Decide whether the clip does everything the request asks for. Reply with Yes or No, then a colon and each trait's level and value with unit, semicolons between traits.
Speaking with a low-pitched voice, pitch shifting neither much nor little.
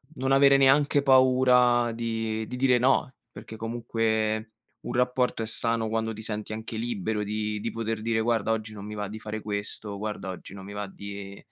No: low, 110 Hz; narrow, 2.3 semitones